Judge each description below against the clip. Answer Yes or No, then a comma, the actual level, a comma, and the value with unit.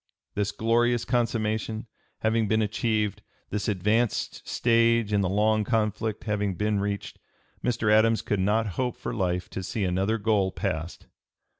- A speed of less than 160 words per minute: Yes, average, 145 wpm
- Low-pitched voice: Yes, low, 110 Hz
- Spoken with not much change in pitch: Yes, narrow, 2.0 semitones